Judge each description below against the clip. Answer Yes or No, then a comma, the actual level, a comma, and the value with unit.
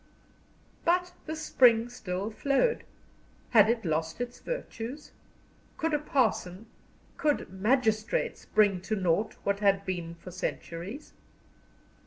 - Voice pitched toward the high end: Yes, high, 220 Hz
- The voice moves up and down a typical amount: No, wide, 6.4 semitones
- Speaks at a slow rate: Yes, slow, 115 wpm